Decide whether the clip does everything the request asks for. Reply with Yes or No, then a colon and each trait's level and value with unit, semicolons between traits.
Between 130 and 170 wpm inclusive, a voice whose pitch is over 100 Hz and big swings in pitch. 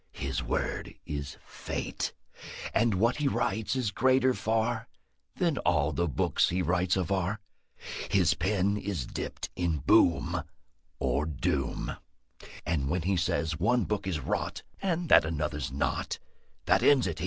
No: average, 145 wpm; very low, 95 Hz; wide, 6.1 semitones